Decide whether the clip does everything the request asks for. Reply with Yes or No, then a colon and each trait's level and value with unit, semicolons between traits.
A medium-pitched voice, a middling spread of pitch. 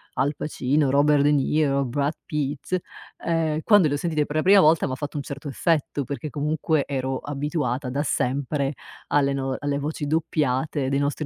No: medium, 145 Hz; narrow, 1.9 semitones